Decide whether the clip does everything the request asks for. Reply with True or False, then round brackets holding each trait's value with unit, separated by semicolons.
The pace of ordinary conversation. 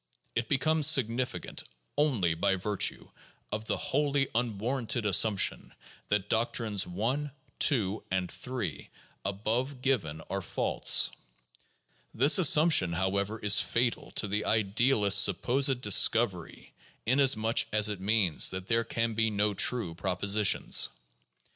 False (115 wpm)